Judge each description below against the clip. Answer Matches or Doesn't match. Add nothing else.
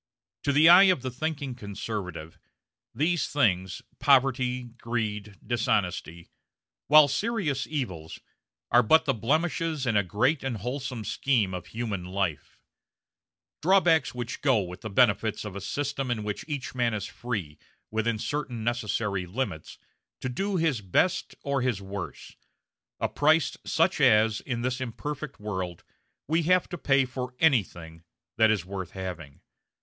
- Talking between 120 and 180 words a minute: Matches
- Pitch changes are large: Matches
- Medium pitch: Doesn't match